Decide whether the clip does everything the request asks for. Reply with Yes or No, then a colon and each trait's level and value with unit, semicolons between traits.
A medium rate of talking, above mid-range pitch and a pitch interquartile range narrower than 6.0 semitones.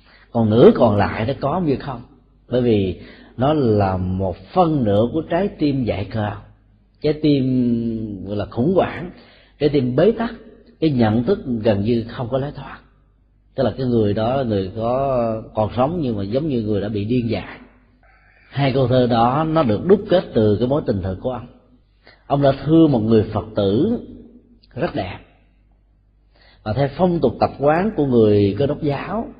No: average, 190 wpm; low, 120 Hz; average, 5.3 semitones